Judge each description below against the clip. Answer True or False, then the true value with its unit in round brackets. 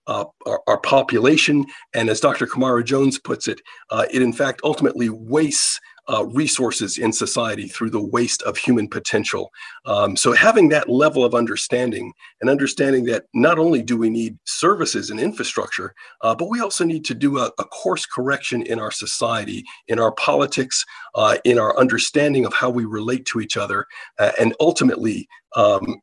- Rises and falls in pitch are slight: False (3.3 semitones)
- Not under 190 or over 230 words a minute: False (175 wpm)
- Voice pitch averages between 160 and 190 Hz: False (130 Hz)